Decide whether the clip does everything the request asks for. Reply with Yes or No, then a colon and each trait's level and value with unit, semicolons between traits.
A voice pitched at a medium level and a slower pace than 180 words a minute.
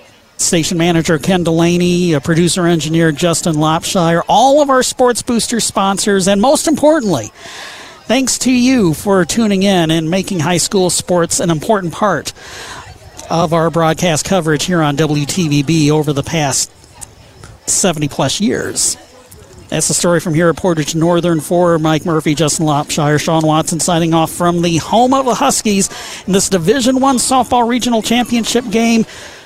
Yes: medium, 175 Hz; average, 155 wpm